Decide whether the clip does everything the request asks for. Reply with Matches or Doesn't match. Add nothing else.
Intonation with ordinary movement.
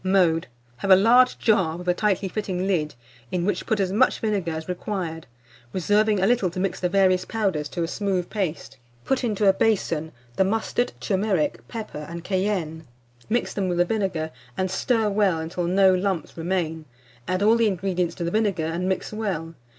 Matches